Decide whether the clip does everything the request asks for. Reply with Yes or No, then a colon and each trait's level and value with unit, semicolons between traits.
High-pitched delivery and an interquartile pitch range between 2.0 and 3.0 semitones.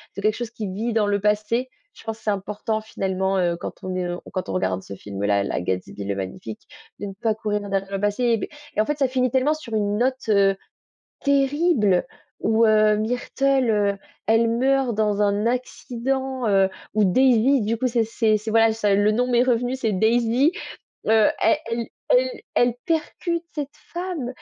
No: high, 220 Hz; average, 3.9 semitones